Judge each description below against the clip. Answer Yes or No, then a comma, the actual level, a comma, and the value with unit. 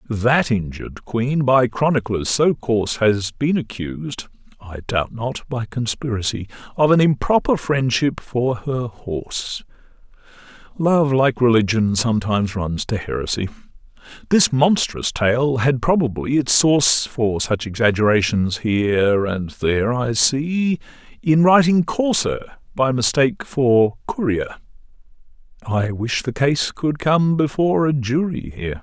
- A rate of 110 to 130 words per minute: Yes, slow, 125 wpm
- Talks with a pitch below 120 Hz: No, low, 125 Hz